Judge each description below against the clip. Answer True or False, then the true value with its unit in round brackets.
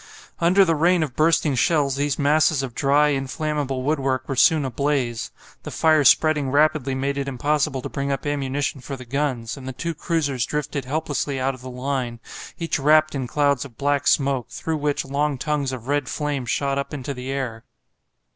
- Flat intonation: True (2.2 semitones)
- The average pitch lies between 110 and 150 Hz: True (140 Hz)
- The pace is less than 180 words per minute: False (190 wpm)